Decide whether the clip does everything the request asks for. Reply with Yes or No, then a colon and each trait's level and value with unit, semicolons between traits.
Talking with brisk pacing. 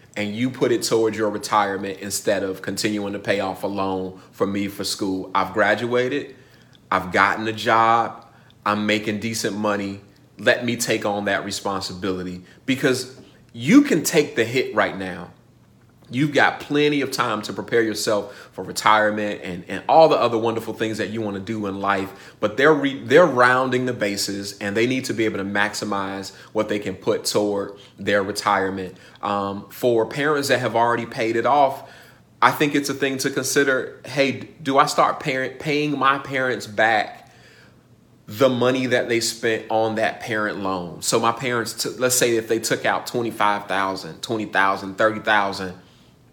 No: average, 175 wpm